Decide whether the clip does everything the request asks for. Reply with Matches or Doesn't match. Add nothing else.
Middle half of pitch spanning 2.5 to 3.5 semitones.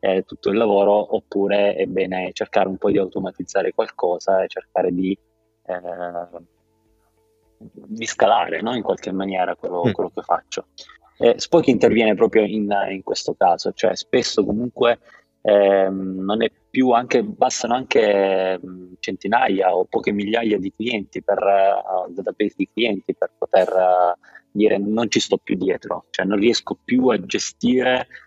Matches